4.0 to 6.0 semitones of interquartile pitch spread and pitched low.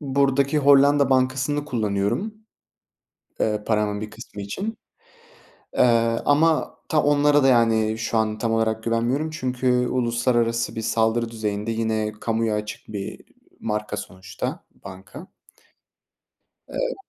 Yes: average, 4.4 semitones; low, 115 Hz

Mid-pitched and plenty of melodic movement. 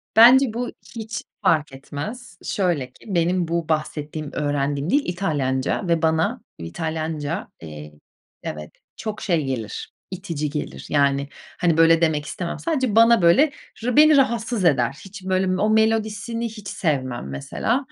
Yes: medium, 170 Hz; wide, 6.9 semitones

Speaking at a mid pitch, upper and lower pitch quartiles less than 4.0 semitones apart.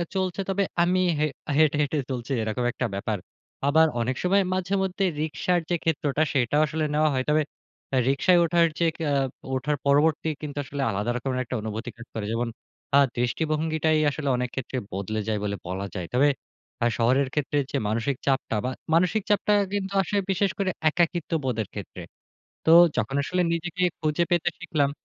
No: medium, 150 Hz; average, 5.3 semitones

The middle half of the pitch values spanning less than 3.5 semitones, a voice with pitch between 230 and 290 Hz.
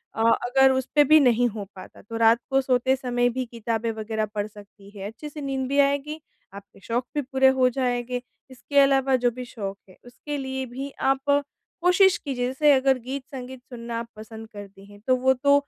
Yes: average, 2.9 semitones; very high, 255 Hz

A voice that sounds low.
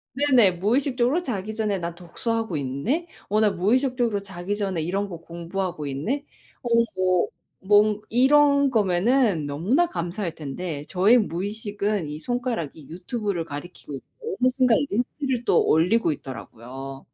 No: high, 200 Hz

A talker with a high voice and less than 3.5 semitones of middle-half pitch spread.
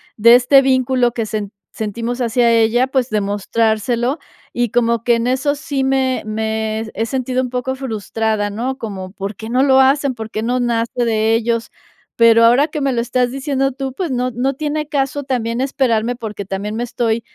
Yes: high, 240 Hz; average, 2.9 semitones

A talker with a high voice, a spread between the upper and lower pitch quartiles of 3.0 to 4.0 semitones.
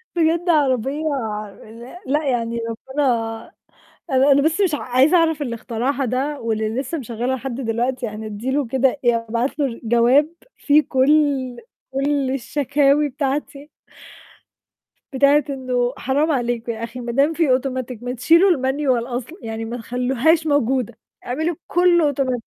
Yes: very high, 265 Hz; average, 3.4 semitones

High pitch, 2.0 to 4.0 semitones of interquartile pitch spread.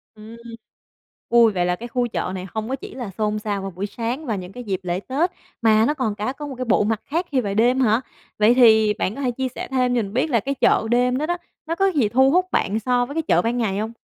Yes: high, 235 Hz; average, 3.6 semitones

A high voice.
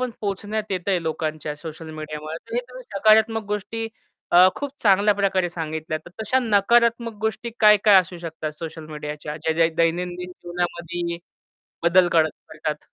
No: medium, 180 Hz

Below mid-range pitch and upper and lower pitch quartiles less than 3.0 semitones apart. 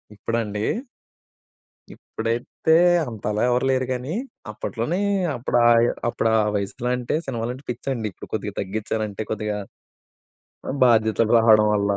Yes: low, 115 Hz; narrow, 2.4 semitones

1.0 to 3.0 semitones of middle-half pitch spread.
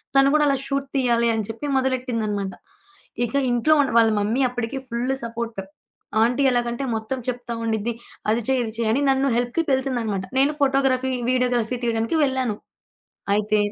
Yes: average, 2.7 semitones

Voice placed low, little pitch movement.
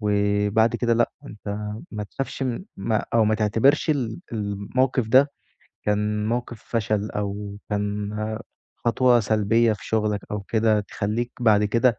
Yes: low, 110 Hz; narrow, 2.3 semitones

